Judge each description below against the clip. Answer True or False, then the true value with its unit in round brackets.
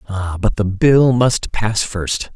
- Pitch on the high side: False (105 Hz)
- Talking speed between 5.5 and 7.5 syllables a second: False (3.3 syllables/s)